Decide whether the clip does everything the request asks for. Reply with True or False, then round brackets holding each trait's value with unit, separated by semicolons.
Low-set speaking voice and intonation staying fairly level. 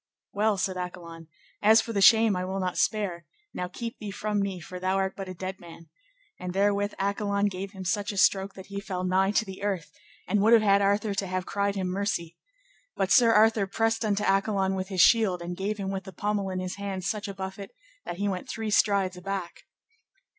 False (195 Hz; 1.8 semitones)